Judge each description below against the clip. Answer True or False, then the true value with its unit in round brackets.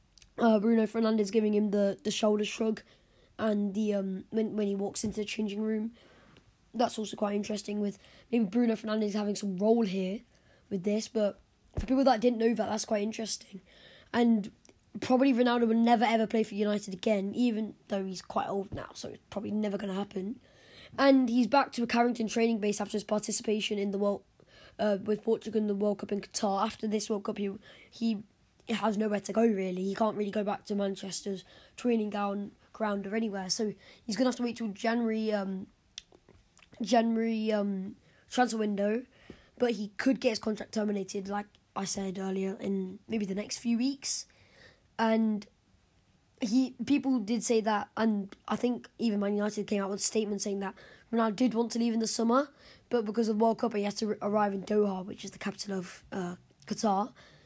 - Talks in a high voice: True (215 Hz)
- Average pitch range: False (2.0 semitones)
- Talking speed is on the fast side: False (195 wpm)